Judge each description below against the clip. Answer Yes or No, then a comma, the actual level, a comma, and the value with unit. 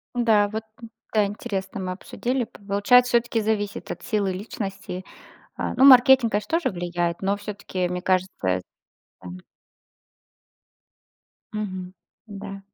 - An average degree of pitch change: Yes, average, 3.2 semitones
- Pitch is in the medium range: No, high, 205 Hz